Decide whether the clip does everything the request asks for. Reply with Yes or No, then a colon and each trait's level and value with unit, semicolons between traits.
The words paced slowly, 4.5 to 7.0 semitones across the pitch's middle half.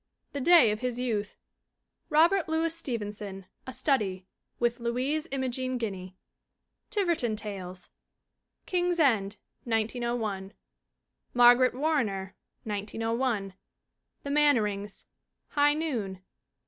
Yes: slow, 95 wpm; wide, 5.6 semitones